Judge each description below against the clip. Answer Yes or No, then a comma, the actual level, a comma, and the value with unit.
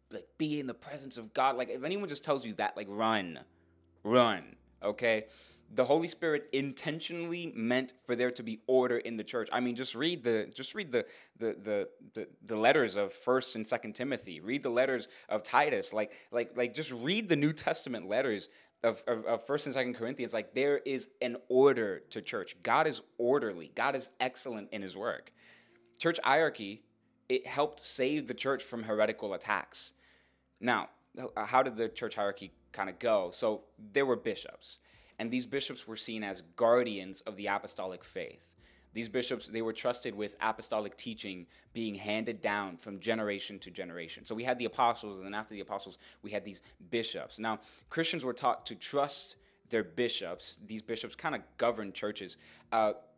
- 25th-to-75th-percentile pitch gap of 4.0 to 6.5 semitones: No, average, 3.6 semitones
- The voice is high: No, low, 115 Hz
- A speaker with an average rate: Yes, average, 185 wpm